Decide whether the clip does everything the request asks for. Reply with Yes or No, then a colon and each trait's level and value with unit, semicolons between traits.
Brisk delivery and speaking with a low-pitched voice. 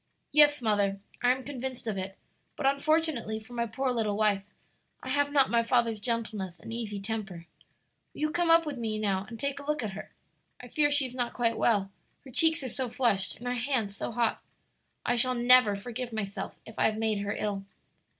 No: fast, 210 wpm; high, 235 Hz